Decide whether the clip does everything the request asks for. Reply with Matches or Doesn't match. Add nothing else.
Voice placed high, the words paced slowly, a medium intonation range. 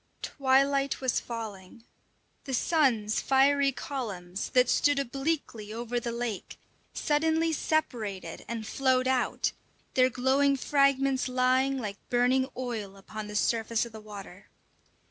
Matches